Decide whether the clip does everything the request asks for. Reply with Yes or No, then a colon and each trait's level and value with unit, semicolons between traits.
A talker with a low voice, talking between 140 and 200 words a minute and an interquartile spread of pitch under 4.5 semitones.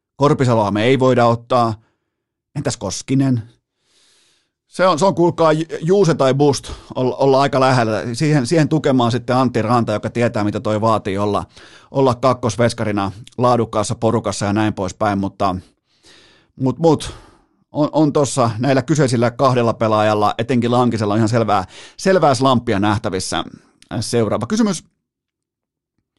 No: low, 120 Hz; average, 130 wpm; average, 3.8 semitones